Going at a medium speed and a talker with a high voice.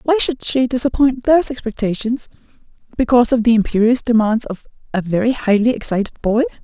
Yes: average, 155 wpm; high, 240 Hz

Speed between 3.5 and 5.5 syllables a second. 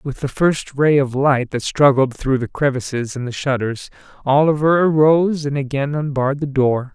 Yes: 4.9 syllables/s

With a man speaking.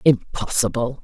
No: female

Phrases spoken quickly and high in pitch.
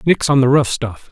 No: fast, 270 wpm; low, 135 Hz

